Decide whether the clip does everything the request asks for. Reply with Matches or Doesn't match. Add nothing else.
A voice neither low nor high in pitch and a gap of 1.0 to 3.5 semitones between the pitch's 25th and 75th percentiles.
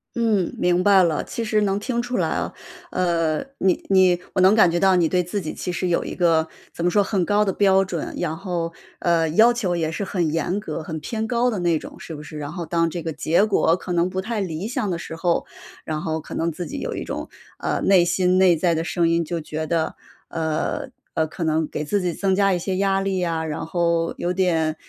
Matches